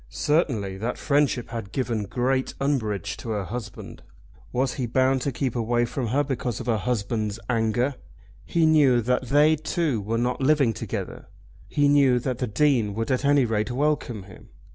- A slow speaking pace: No, average, 175 wpm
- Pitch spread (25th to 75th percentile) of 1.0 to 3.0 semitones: No, average, 3.8 semitones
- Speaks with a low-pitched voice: Yes, low, 125 Hz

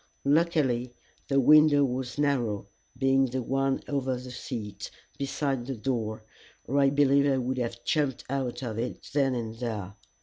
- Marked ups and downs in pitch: No, narrow, 2.6 semitones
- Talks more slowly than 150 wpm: No, average, 160 wpm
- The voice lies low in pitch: Yes, low, 130 Hz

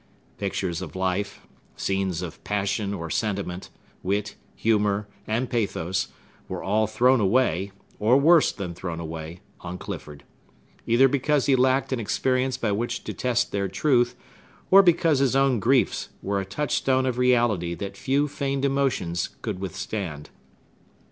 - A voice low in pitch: Yes, low, 110 Hz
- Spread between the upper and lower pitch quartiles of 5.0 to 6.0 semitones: Yes, wide, 5.4 semitones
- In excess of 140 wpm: Yes, average, 150 wpm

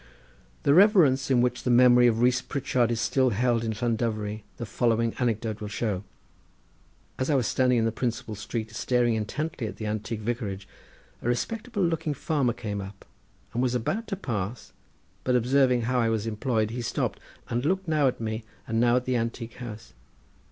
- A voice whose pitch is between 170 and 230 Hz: No, low, 120 Hz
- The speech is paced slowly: No, average, 185 wpm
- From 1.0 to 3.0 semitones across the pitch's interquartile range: Yes, narrow, 2.6 semitones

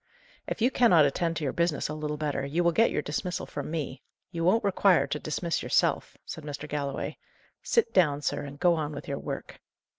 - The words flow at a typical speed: No, fast, 210 wpm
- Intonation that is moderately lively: Yes, average, 3.3 semitones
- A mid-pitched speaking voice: Yes, medium, 155 Hz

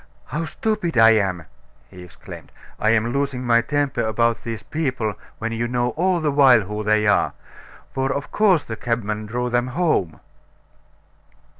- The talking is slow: No, average, 155 wpm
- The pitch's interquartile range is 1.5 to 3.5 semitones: No, average, 4.5 semitones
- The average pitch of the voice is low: Yes, low, 120 Hz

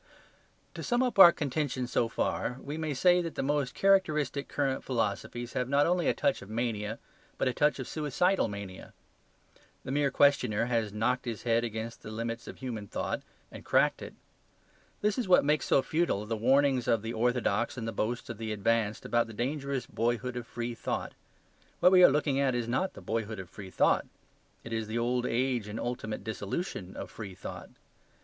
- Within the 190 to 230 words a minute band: Yes, average, 195 wpm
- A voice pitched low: Yes, low, 120 Hz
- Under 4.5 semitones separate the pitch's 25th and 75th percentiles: Yes, average, 4.1 semitones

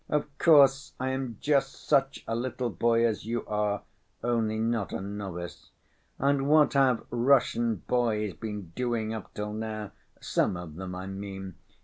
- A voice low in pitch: Yes, low, 115 Hz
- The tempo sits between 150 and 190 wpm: Yes, average, 155 wpm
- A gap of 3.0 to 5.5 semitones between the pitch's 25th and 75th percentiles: Yes, average, 4.2 semitones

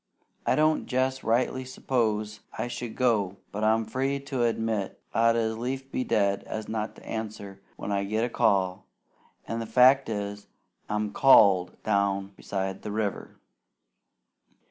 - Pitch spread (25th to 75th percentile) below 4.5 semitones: Yes, average, 3.5 semitones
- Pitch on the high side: No, low, 110 Hz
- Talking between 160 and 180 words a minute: No, average, 150 wpm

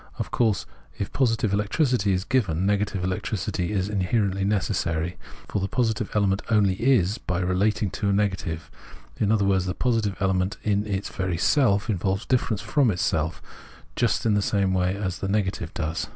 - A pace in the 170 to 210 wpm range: Yes, average, 175 wpm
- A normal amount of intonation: No, narrow, 2.3 semitones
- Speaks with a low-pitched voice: Yes, low, 100 Hz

